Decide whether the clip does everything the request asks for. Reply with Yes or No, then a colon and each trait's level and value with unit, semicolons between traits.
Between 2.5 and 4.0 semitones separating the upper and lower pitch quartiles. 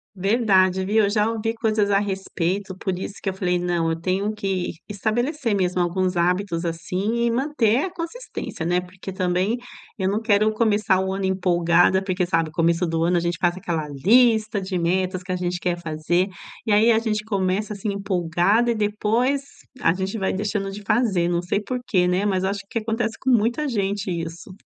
Yes: average, 3.2 semitones